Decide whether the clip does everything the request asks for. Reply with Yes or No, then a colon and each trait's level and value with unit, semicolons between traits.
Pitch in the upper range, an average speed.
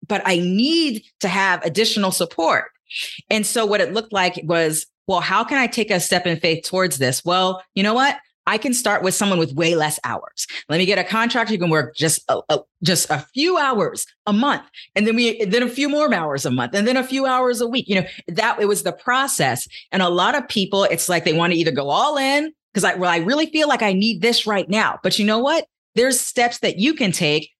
No: high, 205 Hz; fast, 250 wpm